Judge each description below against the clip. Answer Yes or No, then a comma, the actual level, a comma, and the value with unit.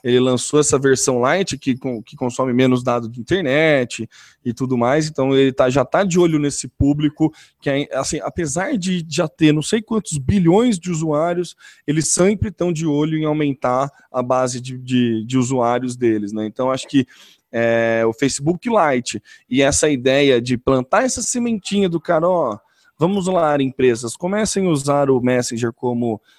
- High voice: No, medium, 140 Hz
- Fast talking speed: No, average, 175 wpm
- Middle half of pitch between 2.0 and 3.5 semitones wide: No, average, 5.1 semitones